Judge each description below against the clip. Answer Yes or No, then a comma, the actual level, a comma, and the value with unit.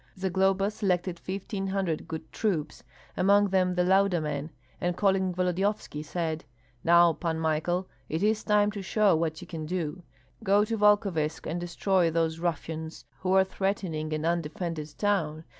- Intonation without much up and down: No, average, 3.3 semitones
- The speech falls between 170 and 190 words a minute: No, average, 155 wpm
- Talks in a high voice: No, medium, 180 Hz